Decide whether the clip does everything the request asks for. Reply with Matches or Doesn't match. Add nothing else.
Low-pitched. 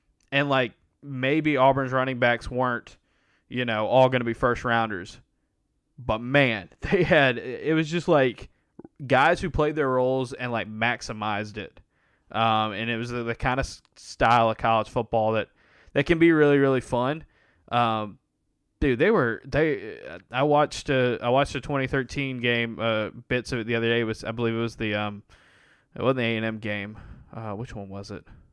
Matches